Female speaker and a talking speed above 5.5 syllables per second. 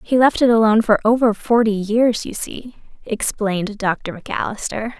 No: female; 5.0 syllables/s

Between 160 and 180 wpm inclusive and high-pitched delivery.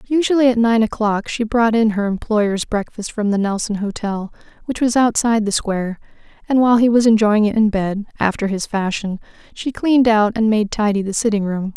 No: average, 200 wpm; high, 215 Hz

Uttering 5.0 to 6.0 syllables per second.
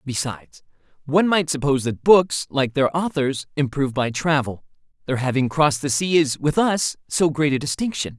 Yes: 5.3 syllables/s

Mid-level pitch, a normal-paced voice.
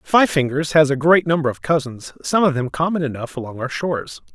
No: medium, 150 Hz; fast, 220 wpm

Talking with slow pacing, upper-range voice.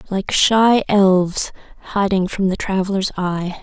Yes: slow, 130 wpm; high, 195 Hz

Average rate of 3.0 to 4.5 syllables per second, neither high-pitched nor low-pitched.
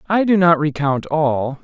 Yes: 4.0 syllables/s; medium, 160 Hz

